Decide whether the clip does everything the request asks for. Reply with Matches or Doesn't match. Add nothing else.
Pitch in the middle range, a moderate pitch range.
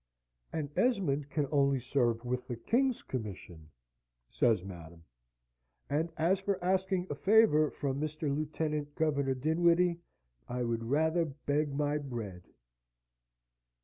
Matches